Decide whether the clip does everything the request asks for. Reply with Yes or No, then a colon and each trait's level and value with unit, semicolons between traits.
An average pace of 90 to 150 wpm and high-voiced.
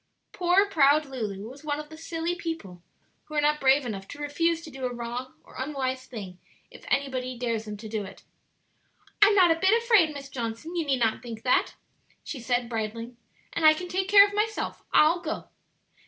No: average, 200 wpm; very high, 280 Hz